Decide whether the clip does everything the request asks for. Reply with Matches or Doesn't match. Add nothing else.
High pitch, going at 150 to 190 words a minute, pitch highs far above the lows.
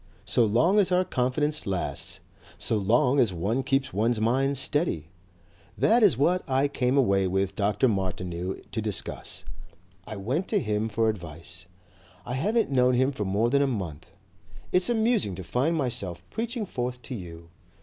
Doesn't match